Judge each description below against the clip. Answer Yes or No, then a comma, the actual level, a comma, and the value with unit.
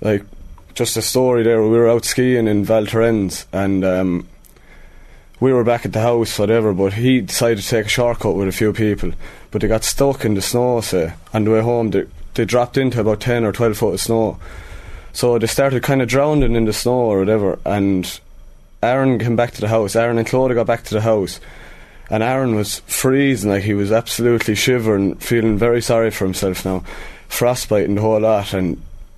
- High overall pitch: No, low, 110 Hz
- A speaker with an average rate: No, fast, 210 wpm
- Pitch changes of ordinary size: Yes, average, 3.3 semitones